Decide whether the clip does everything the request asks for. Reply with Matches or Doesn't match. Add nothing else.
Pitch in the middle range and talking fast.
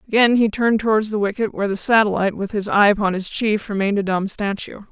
Doesn't match